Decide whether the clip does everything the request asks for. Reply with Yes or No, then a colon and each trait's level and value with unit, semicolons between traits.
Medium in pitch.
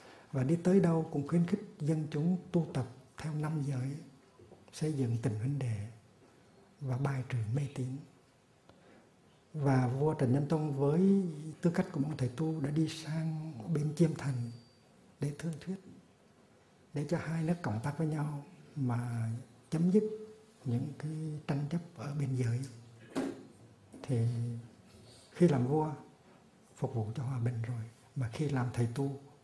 Yes: medium, 145 Hz